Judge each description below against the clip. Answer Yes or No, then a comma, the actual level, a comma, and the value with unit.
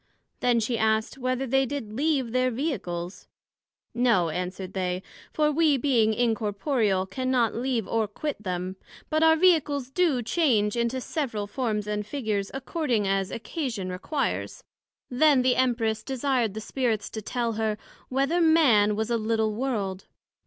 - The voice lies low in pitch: No, high, 235 Hz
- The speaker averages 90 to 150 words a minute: Yes, average, 145 wpm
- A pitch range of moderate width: Yes, average, 4.3 semitones